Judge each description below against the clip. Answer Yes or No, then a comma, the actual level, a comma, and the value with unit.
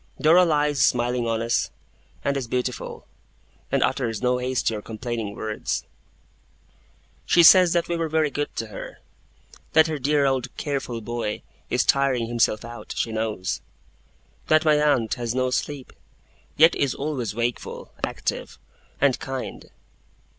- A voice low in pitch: Yes, low, 125 Hz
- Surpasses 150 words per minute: No, average, 145 wpm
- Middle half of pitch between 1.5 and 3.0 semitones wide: No, average, 4.1 semitones